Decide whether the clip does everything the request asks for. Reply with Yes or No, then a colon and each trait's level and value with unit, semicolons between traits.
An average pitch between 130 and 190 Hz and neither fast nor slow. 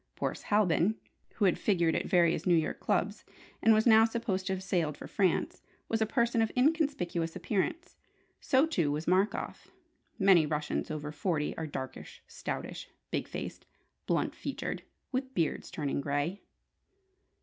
Yes: medium, 185 Hz; average, 150 wpm